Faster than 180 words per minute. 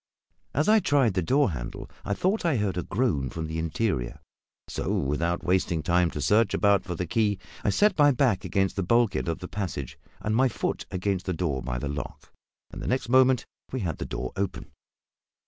Yes: fast, 205 wpm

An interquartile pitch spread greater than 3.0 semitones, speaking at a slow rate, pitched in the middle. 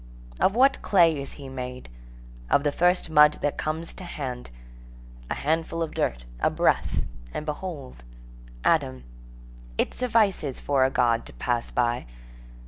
No: average, 4.9 semitones; average, 145 wpm; medium, 145 Hz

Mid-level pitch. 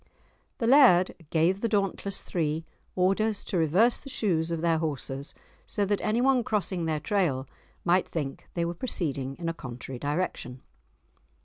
Yes: medium, 175 Hz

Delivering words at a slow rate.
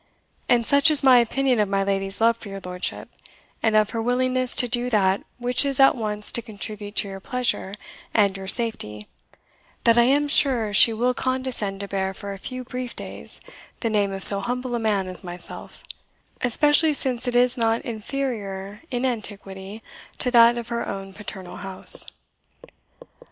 No: average, 180 wpm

